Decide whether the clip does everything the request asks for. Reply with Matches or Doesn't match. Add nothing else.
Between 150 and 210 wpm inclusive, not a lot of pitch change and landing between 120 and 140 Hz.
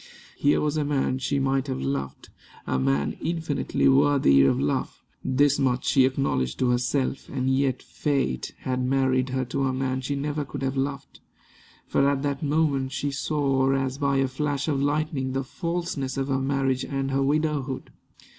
Matches